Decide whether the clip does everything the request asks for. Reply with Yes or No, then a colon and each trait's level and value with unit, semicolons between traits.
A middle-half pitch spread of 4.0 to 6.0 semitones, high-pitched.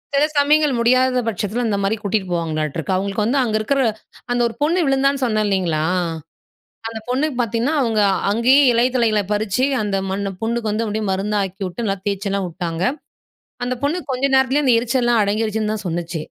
Yes: average, 4.3 semitones; high, 220 Hz